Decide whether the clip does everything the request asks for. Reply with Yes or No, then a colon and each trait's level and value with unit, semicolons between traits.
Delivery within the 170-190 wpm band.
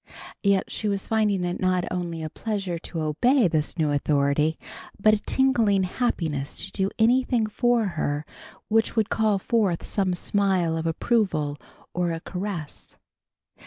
No: average, 150 wpm